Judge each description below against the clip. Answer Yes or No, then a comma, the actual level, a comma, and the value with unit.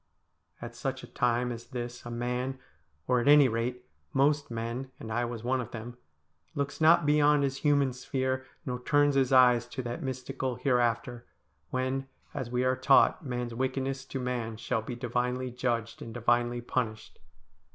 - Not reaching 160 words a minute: No, average, 175 wpm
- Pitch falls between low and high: No, low, 125 Hz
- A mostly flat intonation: Yes, narrow, 1.8 semitones